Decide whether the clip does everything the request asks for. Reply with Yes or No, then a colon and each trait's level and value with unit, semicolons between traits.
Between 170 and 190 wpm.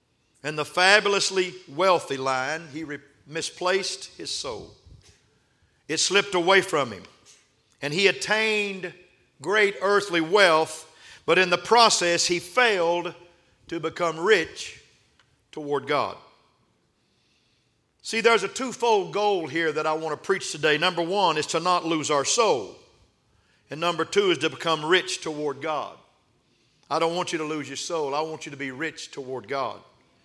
No: average, 155 wpm